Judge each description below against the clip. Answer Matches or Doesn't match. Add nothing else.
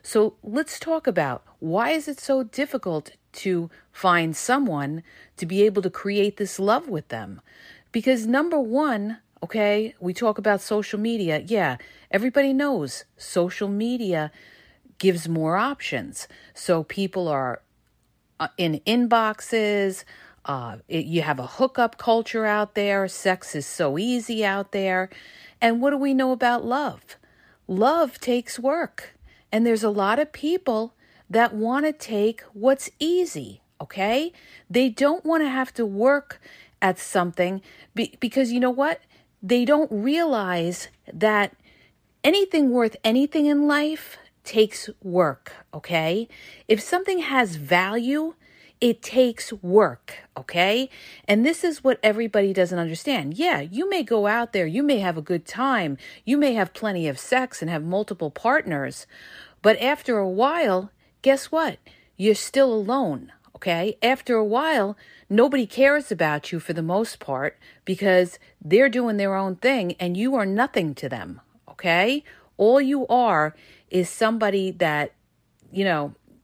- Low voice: Doesn't match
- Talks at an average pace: Matches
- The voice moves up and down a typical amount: Doesn't match